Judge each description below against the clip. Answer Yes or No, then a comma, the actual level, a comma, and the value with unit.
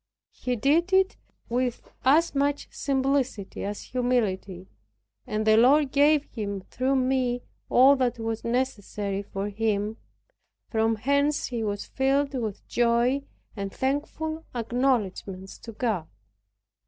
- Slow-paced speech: Yes, slow, 120 wpm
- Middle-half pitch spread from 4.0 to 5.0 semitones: Yes, average, 4.4 semitones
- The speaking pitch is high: Yes, high, 245 Hz